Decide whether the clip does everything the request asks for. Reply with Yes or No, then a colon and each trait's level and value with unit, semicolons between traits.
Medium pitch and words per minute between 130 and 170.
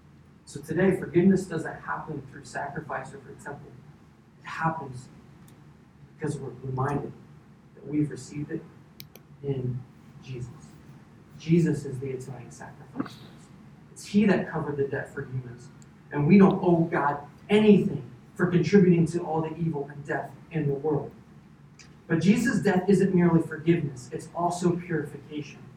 Yes: medium, 155 Hz; average, 140 wpm